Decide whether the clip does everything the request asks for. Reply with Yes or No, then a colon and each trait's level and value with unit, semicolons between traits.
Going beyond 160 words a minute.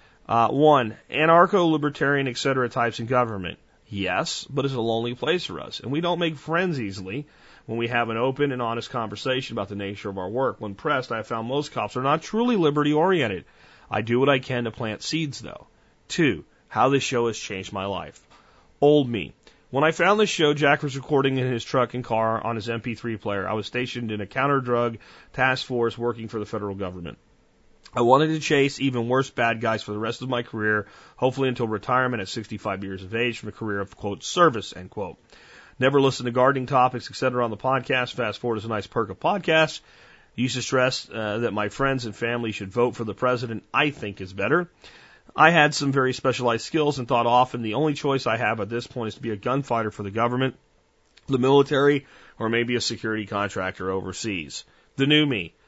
Yes: average, 215 wpm